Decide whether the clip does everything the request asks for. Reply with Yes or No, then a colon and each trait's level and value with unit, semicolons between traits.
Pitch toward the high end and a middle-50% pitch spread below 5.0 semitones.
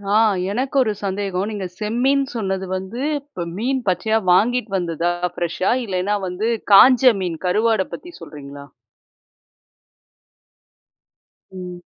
Yes: high, 200 Hz; average, 4.4 semitones